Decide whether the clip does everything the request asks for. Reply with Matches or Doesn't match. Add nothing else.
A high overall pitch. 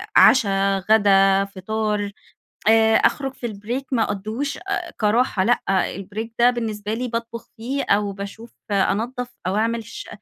Matches